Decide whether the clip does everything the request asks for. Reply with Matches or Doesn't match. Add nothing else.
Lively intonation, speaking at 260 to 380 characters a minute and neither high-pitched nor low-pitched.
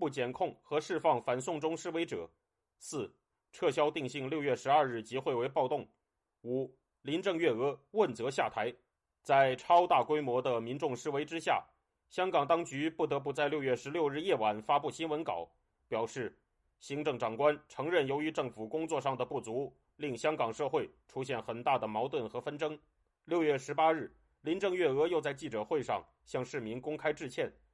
Doesn't match